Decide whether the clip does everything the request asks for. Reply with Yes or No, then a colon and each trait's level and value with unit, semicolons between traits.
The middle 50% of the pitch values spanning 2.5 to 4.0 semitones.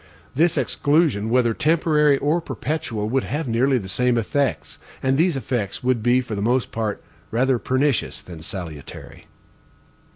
No: average, 4.4 semitones